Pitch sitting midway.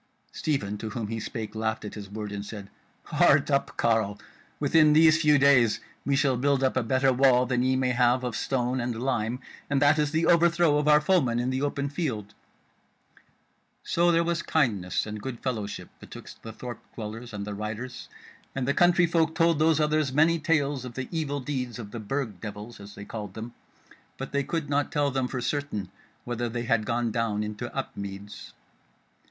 No: low, 125 Hz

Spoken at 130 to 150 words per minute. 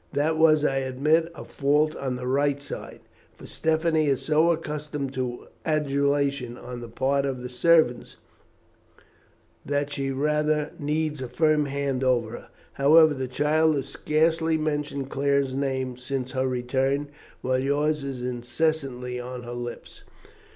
Yes: average, 145 wpm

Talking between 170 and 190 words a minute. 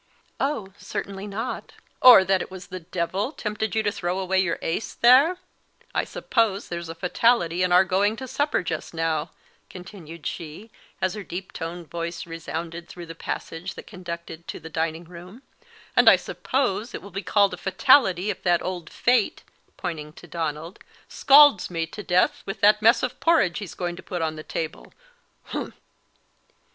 Yes: average, 175 wpm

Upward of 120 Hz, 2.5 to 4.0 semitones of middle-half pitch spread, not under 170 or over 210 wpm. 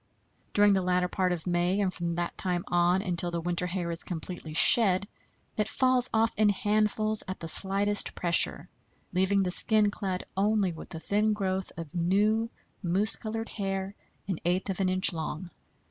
Yes: high, 190 Hz; average, 2.8 semitones; average, 180 wpm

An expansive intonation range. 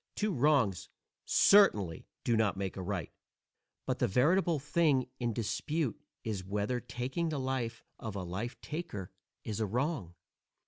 Yes: wide, 6.7 semitones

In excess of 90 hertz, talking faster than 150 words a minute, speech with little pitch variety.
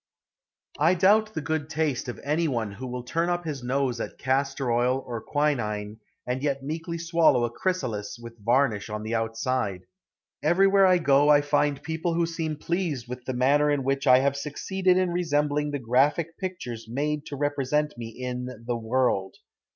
No: medium, 140 Hz; average, 180 wpm; average, 4.5 semitones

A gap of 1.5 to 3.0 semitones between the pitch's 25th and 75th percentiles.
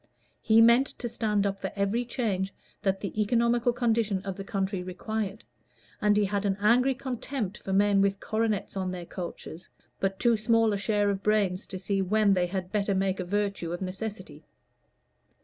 Yes: narrow, 2.4 semitones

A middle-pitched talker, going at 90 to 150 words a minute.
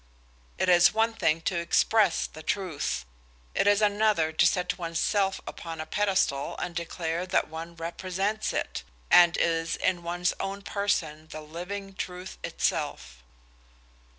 Yes: medium, 175 Hz; average, 145 wpm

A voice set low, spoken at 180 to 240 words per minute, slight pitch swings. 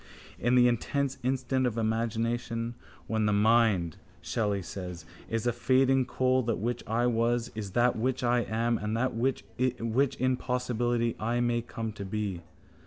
No: low, 120 Hz; average, 160 wpm; narrow, 2.0 semitones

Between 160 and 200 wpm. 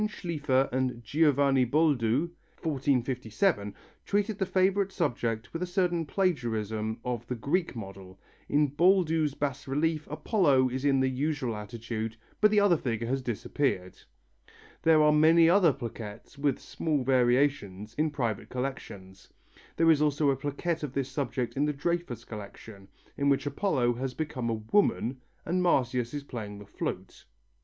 No: average, 150 wpm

